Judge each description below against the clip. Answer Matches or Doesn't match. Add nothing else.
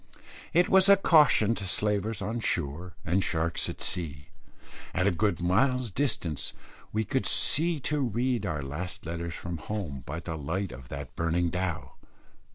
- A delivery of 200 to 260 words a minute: Doesn't match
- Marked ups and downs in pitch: Matches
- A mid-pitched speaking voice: Doesn't match